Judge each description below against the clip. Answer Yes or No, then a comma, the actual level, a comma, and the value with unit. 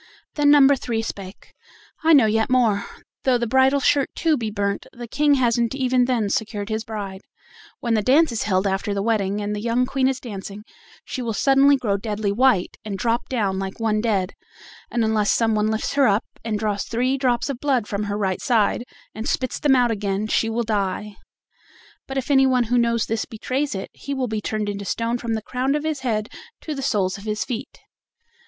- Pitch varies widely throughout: No, average, 3.8 semitones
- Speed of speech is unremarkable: No, fast, 210 wpm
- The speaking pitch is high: Yes, high, 225 Hz